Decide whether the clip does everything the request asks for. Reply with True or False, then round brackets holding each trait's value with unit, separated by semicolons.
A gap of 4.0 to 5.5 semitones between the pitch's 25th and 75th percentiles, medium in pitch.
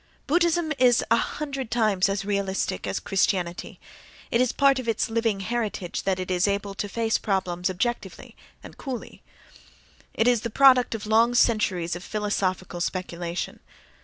False (4.4 semitones; 210 Hz)